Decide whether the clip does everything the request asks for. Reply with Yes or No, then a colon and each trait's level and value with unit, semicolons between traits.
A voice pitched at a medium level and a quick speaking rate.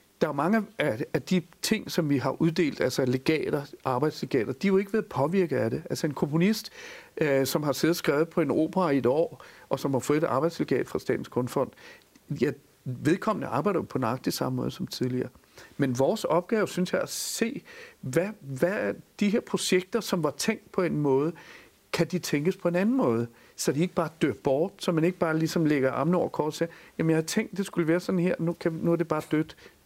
Yes: medium, 170 Hz; fast, 230 wpm